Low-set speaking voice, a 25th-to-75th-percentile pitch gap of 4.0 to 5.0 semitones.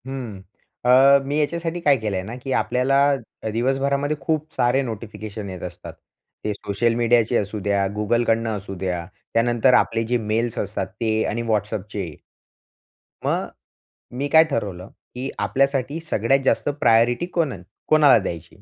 Yes: low, 120 Hz; average, 4.4 semitones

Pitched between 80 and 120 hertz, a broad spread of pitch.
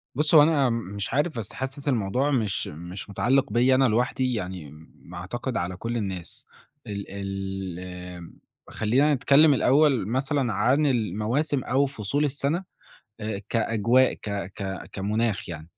Yes: low, 115 Hz; wide, 5.8 semitones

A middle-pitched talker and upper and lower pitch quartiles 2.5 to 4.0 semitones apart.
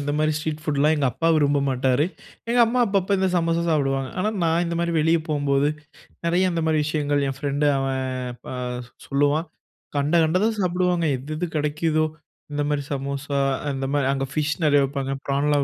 Yes: medium, 150 Hz; average, 3.0 semitones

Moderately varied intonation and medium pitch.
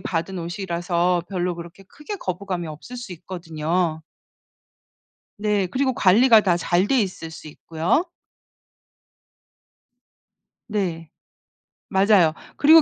Yes: average, 3.4 semitones; medium, 180 Hz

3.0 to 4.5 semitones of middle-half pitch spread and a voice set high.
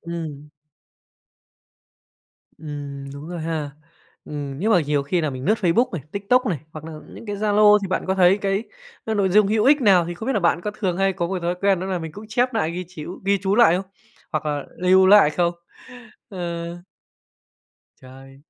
No: average, 4.2 semitones; medium, 180 Hz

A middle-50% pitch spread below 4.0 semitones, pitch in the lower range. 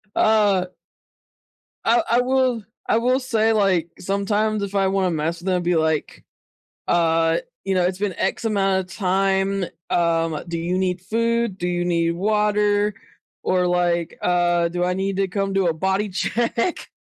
No: average, 3.0 semitones; high, 190 Hz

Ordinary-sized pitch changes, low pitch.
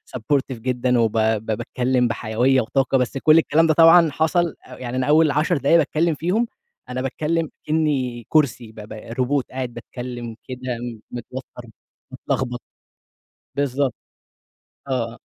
Yes: average, 4.0 semitones; low, 130 Hz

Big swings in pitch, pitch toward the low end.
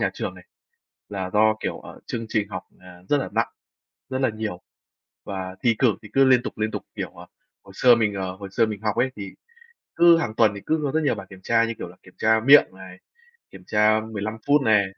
No: average, 3.4 semitones; low, 110 Hz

